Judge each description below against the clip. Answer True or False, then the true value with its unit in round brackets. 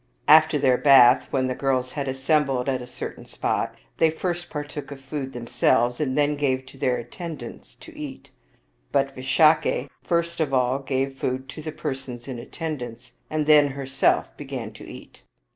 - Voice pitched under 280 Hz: True (135 Hz)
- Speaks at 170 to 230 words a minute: True (175 wpm)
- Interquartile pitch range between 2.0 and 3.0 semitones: True (2.6 semitones)